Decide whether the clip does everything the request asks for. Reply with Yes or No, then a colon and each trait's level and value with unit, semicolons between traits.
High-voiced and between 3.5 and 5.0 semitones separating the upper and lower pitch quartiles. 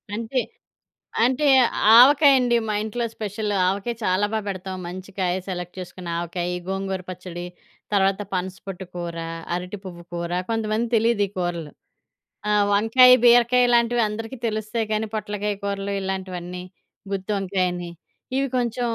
Yes: high, 200 Hz; average, 3.8 semitones